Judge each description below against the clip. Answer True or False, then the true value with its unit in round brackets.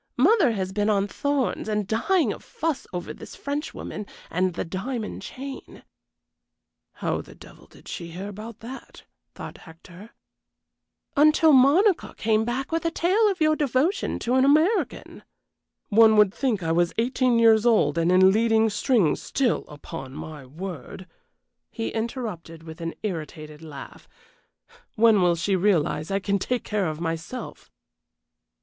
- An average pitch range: False (6.7 semitones)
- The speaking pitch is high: True (215 Hz)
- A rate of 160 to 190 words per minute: False (150 wpm)